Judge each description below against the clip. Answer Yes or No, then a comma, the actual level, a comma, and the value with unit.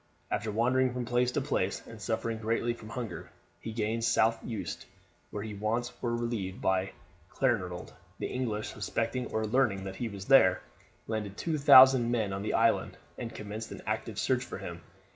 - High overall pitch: No, low, 115 Hz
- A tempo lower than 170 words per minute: No, average, 180 wpm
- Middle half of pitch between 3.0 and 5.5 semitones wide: No, narrow, 2.6 semitones